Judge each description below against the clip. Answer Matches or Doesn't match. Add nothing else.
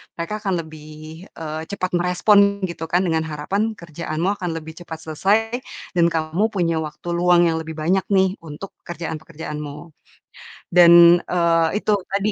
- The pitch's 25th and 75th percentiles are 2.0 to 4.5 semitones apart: Matches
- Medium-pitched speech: Matches